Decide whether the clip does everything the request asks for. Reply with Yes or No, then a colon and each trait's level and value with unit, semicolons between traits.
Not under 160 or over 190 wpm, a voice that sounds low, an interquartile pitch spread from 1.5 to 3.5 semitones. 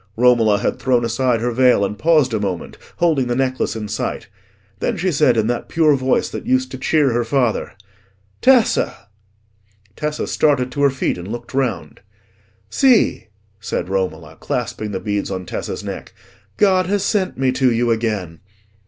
No: average, 170 wpm; low, 125 Hz; wide, 5.4 semitones